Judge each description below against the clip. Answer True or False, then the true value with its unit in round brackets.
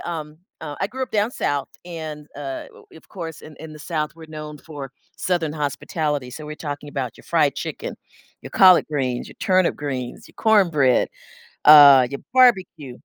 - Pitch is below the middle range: False (150 Hz)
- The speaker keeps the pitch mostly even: False (3.0 semitones)